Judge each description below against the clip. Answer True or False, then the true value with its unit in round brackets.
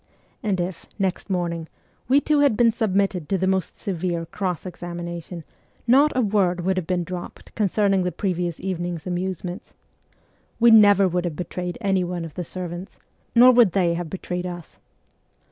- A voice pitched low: False (185 Hz)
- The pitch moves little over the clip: True (2.3 semitones)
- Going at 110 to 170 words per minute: True (165 wpm)